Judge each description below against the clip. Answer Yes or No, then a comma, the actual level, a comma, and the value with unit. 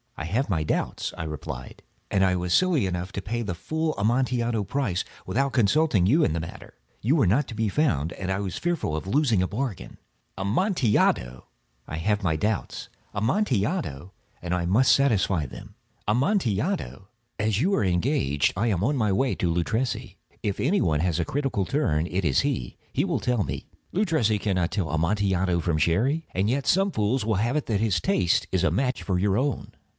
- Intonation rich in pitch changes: Yes, wide, 6.8 semitones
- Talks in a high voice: No, low, 105 Hz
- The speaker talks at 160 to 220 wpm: Yes, average, 190 wpm